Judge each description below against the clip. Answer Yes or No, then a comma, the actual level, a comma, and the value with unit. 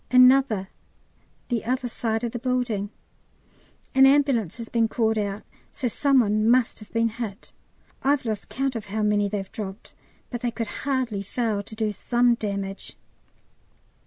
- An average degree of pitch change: Yes, average, 3.2 semitones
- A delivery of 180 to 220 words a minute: No, average, 160 wpm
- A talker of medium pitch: No, high, 230 Hz